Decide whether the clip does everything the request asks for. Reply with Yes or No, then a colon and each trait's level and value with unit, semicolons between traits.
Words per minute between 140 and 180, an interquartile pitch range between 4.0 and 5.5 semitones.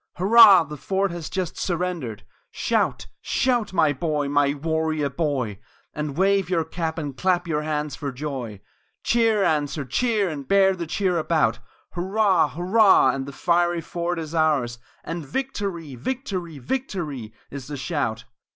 Yes: average, 150 wpm; average, 4.6 semitones